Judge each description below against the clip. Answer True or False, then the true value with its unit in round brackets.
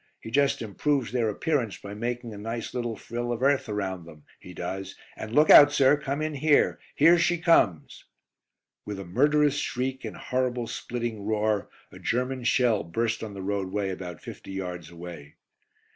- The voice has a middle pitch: False (115 Hz)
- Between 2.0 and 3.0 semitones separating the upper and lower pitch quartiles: False (5.3 semitones)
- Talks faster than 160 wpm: True (175 wpm)